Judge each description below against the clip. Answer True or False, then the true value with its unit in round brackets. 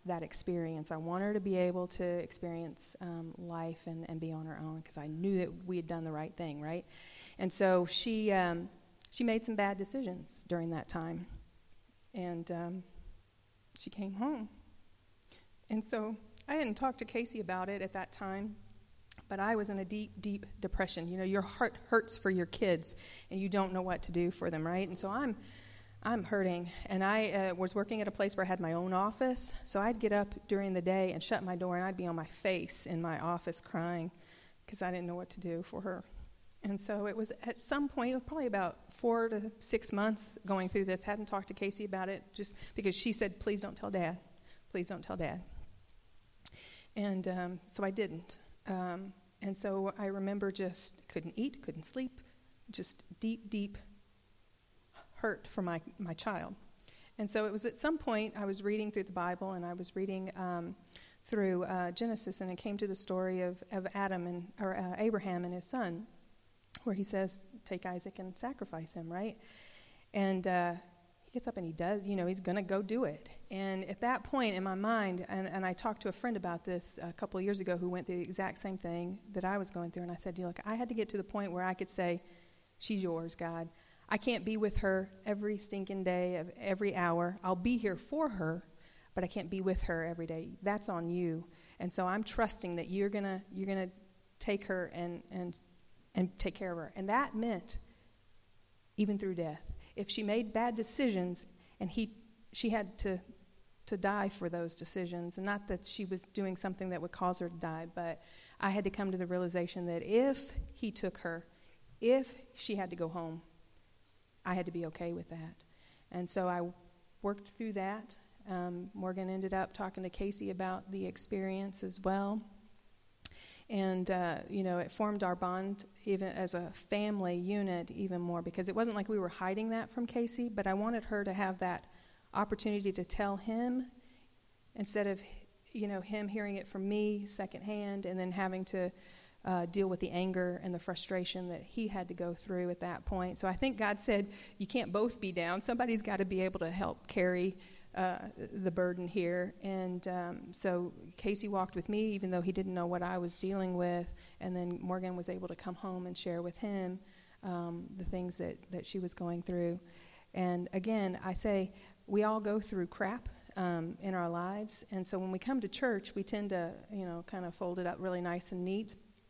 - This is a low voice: False (190 Hz)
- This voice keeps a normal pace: False (210 wpm)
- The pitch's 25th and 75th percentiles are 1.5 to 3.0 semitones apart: True (2.7 semitones)